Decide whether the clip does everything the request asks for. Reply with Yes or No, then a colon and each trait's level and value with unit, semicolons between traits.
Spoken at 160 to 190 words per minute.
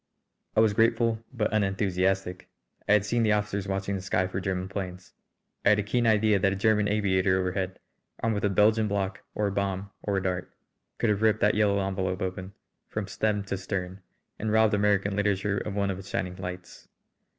No: average, 200 wpm